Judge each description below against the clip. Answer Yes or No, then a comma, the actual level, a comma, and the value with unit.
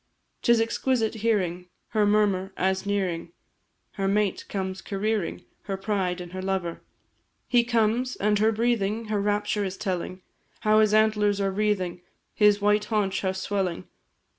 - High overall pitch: Yes, high, 205 Hz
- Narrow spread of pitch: Yes, narrow, 2.2 semitones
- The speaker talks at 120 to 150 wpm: Yes, average, 145 wpm